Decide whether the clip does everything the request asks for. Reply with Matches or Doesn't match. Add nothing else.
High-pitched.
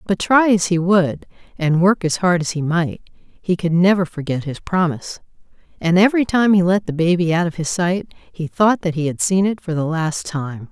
Doesn't match